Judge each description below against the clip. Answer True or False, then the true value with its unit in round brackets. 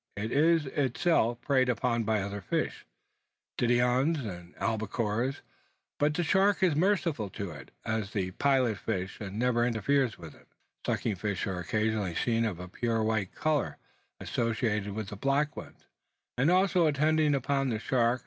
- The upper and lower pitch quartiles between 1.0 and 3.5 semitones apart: False (5.2 semitones)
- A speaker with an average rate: True (160 wpm)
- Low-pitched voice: True (120 Hz)